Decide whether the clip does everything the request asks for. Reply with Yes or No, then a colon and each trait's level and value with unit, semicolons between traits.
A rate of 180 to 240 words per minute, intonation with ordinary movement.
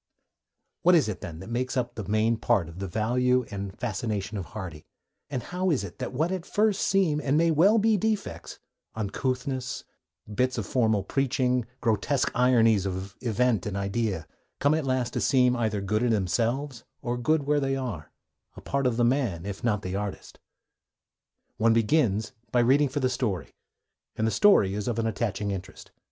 Yes: average, 185 wpm; average, 4.7 semitones